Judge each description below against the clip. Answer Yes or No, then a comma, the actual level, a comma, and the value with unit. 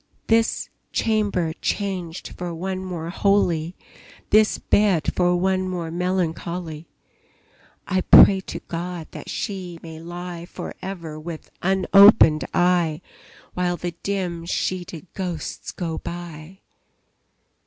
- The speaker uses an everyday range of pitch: No, narrow, 2.2 semitones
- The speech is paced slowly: Yes, slow, 110 wpm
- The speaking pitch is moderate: Yes, medium, 175 Hz